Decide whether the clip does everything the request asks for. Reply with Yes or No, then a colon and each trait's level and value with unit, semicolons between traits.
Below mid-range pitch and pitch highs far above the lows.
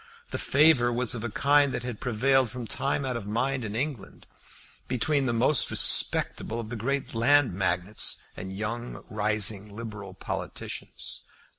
No: low, 120 Hz; average, 3.9 semitones